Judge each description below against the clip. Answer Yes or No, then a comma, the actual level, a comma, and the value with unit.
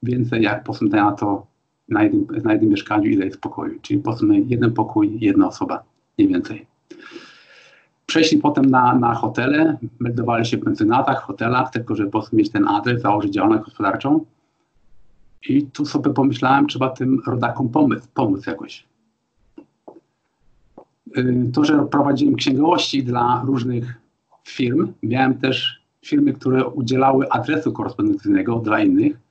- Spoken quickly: No, average, 145 wpm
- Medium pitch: Yes, medium, 150 Hz